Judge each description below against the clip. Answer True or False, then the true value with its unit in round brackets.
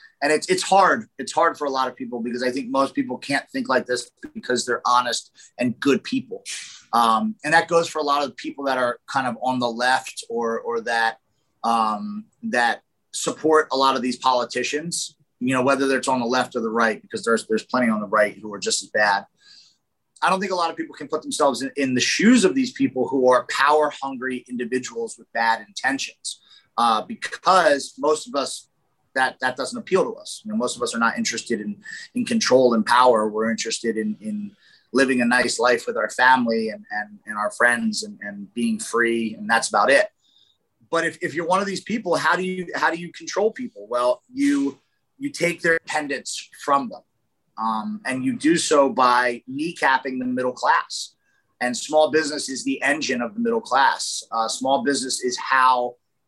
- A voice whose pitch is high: False (135 Hz)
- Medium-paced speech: False (210 wpm)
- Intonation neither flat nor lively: False (6.0 semitones)